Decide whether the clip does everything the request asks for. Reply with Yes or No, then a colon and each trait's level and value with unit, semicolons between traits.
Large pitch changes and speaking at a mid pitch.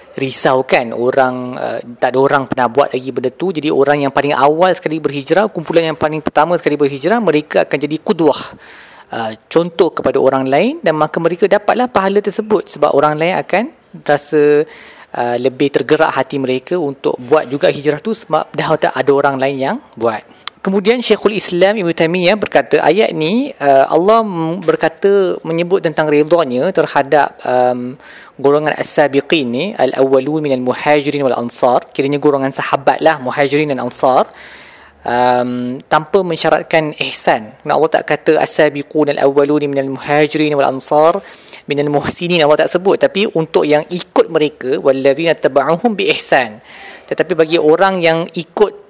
No: average, 3.6 semitones; medium, 150 Hz